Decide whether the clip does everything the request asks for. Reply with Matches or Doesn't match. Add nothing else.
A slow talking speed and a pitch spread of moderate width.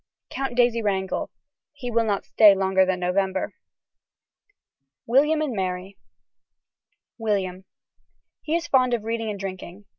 Matches